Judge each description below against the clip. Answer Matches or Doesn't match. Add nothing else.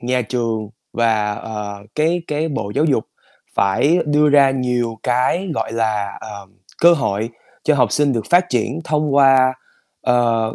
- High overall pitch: Doesn't match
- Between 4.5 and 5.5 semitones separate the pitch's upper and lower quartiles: Matches